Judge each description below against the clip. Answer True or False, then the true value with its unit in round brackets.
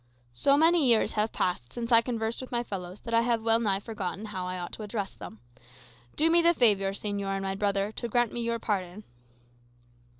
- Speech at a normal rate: False (220 wpm)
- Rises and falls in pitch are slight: False (3.4 semitones)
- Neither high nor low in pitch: False (215 Hz)